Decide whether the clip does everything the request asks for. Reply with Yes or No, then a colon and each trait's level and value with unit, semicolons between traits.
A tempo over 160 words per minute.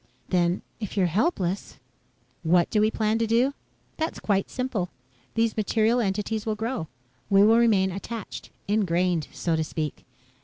No: average, 155 wpm